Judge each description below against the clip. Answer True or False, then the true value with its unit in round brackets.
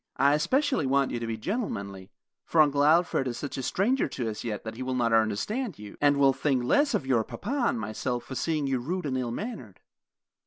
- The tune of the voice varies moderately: False (5.9 semitones)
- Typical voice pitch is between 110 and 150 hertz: True (135 Hz)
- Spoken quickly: True (225 wpm)